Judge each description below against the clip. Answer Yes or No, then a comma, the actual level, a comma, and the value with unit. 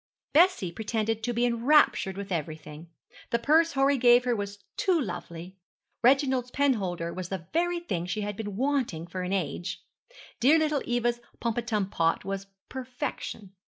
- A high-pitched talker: Yes, high, 225 Hz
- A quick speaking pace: No, average, 155 wpm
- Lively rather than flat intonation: Yes, wide, 5.9 semitones